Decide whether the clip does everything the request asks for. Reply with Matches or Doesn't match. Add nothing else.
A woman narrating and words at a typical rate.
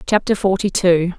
Matches